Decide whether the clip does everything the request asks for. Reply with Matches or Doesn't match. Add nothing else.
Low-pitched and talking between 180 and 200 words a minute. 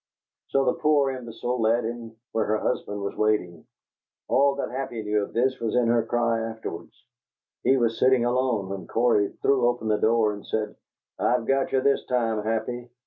Matches